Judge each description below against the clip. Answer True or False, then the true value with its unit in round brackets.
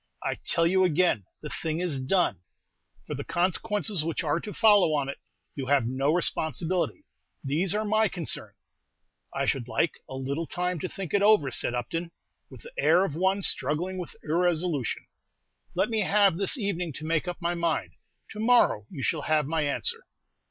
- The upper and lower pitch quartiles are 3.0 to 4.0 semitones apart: False (4.4 semitones)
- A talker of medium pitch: True (170 Hz)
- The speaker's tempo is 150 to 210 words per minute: True (180 wpm)